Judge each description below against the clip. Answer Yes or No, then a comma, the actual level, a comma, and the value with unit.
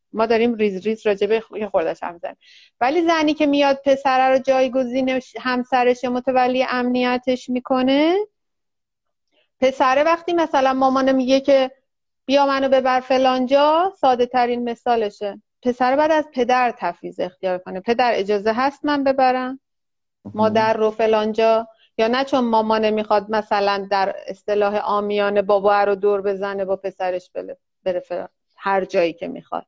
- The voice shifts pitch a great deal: No, average, 4.2 semitones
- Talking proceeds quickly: No, average, 140 wpm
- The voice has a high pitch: Yes, high, 245 Hz